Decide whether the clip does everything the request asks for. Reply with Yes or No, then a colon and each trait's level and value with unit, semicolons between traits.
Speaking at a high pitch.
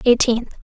Yes: high, 240 Hz